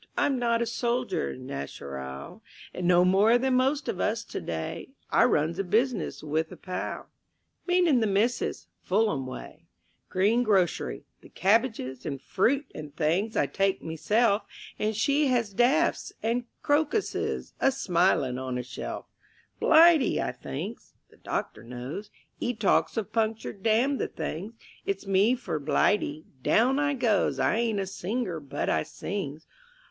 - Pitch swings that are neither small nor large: No, wide, 7.1 semitones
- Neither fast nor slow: Yes, average, 145 wpm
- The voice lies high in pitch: Yes, high, 210 Hz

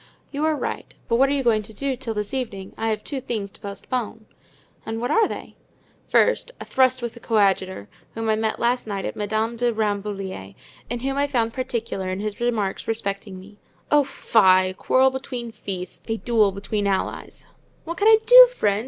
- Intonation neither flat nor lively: Yes, average, 4.2 semitones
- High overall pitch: Yes, high, 225 Hz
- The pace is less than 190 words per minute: No, average, 195 wpm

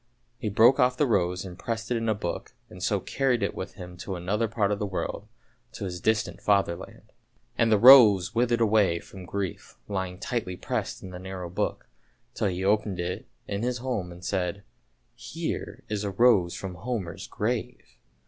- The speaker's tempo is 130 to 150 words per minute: No, average, 195 wpm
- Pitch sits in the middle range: No, low, 100 Hz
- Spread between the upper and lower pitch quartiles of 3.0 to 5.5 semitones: Yes, average, 3.9 semitones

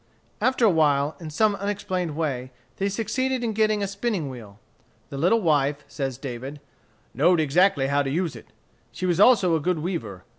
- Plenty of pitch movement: Yes, wide, 6.1 semitones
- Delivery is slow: No, average, 180 wpm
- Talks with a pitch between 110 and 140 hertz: No, medium, 165 Hz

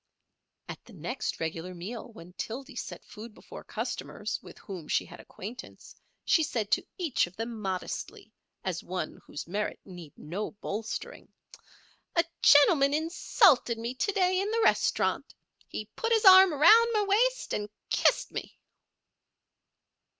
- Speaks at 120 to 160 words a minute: Yes, average, 145 wpm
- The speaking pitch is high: Yes, high, 235 Hz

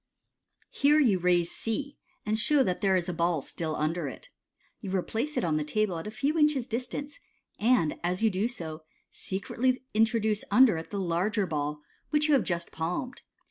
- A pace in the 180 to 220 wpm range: Yes, average, 190 wpm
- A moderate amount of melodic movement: No, wide, 6.6 semitones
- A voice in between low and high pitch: No, high, 210 Hz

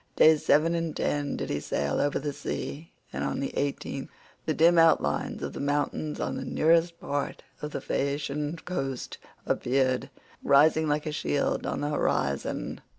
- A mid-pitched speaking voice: Yes, medium, 145 Hz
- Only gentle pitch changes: Yes, narrow, 2.2 semitones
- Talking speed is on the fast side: No, average, 165 wpm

